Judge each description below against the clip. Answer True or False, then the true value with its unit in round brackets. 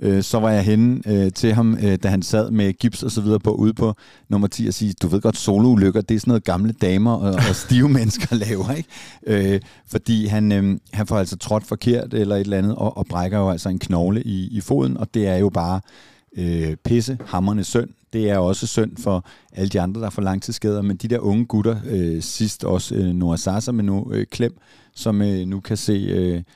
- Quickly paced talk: True (235 wpm)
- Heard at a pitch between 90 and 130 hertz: True (105 Hz)